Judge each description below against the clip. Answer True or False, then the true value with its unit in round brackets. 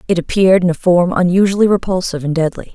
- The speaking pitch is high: False (180 Hz)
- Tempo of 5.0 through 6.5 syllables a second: False (7.0 syllables/s)